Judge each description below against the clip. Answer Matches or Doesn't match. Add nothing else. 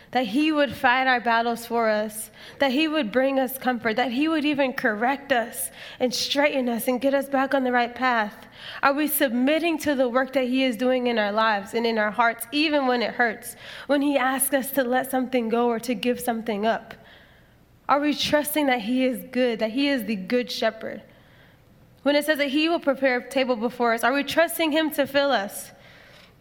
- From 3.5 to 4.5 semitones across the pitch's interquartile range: Doesn't match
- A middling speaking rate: Doesn't match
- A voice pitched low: Doesn't match